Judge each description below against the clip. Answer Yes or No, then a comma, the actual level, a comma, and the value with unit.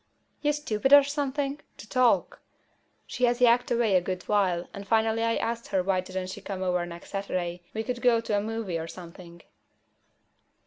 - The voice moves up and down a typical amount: Yes, average, 4.7 semitones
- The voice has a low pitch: No, high, 210 Hz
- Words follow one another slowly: No, average, 185 wpm